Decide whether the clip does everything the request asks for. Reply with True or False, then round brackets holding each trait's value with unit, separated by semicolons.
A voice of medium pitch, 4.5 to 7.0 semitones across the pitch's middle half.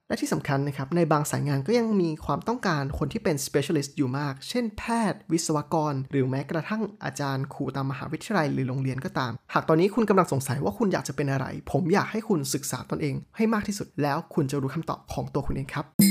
True (150 Hz; 5.1 semitones)